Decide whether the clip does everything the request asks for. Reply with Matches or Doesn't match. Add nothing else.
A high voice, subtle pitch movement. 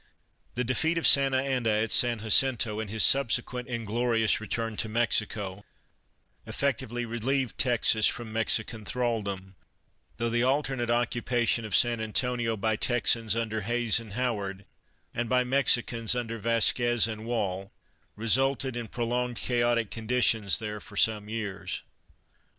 Doesn't match